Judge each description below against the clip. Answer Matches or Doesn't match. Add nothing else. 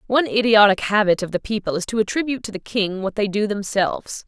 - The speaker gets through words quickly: Matches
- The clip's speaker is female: Matches